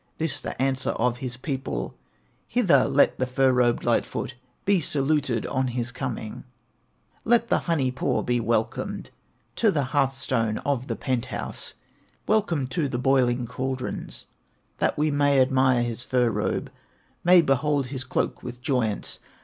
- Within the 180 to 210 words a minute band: No, average, 150 wpm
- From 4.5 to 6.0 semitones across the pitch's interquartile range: No, narrow, 2.6 semitones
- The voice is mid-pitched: No, low, 130 Hz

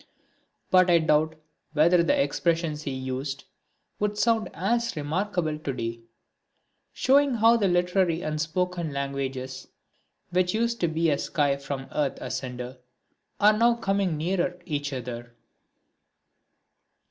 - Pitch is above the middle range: No, medium, 160 Hz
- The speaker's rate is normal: No, slow, 125 wpm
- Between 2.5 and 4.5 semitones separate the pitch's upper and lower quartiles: No, average, 5.2 semitones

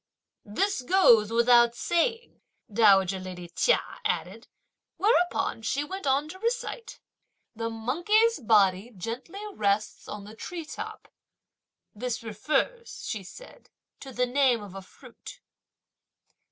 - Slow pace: Yes, slow, 120 wpm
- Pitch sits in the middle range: No, high, 245 Hz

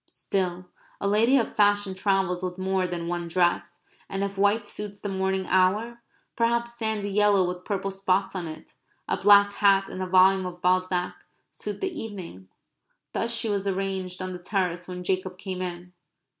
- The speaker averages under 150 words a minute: No, average, 175 wpm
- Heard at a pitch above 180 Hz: Yes, high, 190 Hz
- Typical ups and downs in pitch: No, narrow, 1.9 semitones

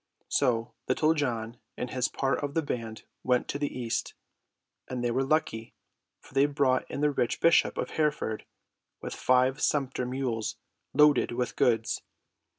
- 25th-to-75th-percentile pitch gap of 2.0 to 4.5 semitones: Yes, average, 3.2 semitones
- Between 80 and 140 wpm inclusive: No, average, 155 wpm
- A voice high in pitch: No, low, 130 Hz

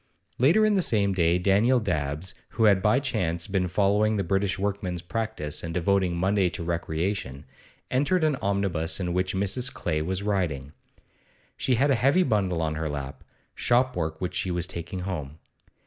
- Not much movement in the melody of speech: No, average, 4.1 semitones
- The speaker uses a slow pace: No, average, 170 wpm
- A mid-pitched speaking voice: No, very low, 95 Hz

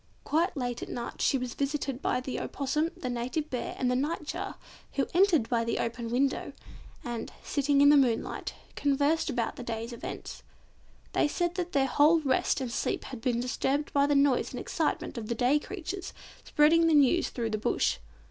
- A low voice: No, very high, 275 Hz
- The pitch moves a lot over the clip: No, average, 3.6 semitones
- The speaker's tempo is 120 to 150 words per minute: No, average, 190 wpm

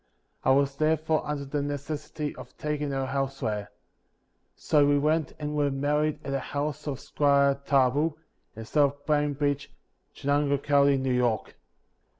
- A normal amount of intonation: No, narrow, 1.4 semitones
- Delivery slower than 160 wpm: Yes, average, 145 wpm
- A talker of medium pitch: Yes, medium, 145 Hz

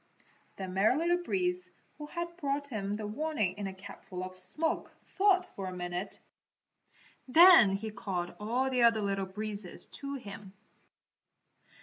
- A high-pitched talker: Yes, high, 215 Hz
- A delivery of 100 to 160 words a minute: Yes, average, 145 wpm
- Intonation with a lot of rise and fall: Yes, wide, 7.5 semitones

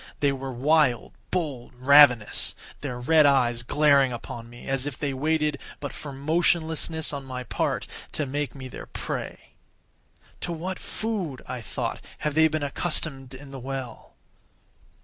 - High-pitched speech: No, medium, 140 Hz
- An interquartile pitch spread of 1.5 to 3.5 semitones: Yes, average, 3.2 semitones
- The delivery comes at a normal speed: Yes, average, 150 wpm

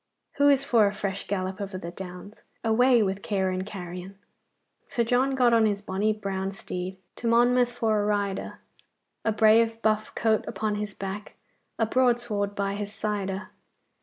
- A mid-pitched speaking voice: No, high, 210 Hz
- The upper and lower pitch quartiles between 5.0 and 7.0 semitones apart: No, average, 2.9 semitones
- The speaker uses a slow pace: No, average, 175 wpm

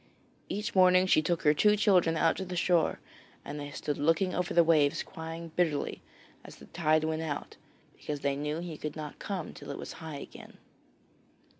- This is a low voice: No, medium, 165 Hz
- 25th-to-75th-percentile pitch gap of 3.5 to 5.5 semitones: No, average, 3.0 semitones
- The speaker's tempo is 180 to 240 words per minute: Yes, average, 190 wpm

